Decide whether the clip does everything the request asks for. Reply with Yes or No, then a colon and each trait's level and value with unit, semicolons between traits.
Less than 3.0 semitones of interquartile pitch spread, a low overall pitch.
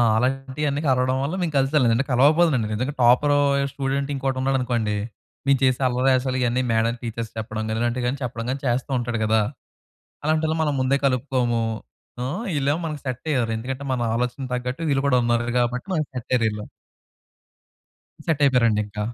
Yes: narrow, 2.6 semitones; low, 130 Hz